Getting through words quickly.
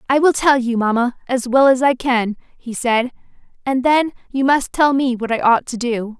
Yes: fast, 225 wpm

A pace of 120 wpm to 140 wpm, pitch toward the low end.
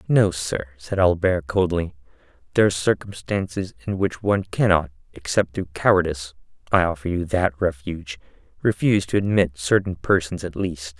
Yes: slow, 135 wpm; very low, 90 Hz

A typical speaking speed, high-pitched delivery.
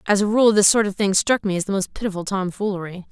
No: fast, 270 wpm; high, 200 Hz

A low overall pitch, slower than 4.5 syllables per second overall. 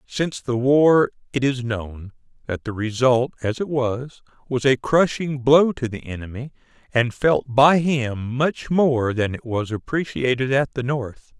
Yes: low, 130 Hz; 4.0 syllables/s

